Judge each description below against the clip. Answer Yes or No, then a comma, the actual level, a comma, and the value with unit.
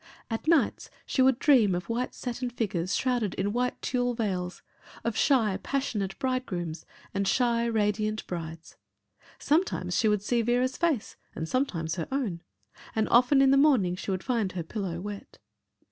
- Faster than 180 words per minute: No, average, 160 wpm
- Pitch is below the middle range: No, high, 225 Hz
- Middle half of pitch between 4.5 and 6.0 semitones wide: Yes, average, 5.1 semitones